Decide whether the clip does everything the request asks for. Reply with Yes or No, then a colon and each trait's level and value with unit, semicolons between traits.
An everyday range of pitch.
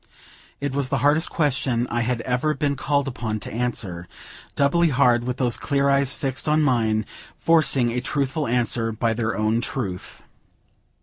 Yes: average, 3.3 semitones